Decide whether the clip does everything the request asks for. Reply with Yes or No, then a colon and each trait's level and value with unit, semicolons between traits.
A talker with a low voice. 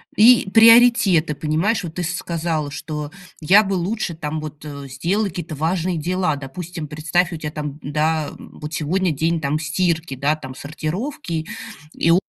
No: medium, 160 Hz